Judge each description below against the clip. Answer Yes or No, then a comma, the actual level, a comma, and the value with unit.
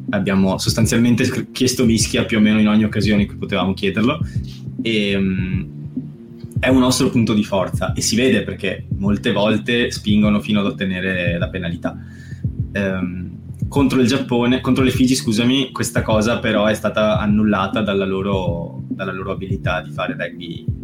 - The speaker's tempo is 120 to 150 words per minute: No, average, 160 wpm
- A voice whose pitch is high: No, low, 110 Hz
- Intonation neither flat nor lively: Yes, average, 3.2 semitones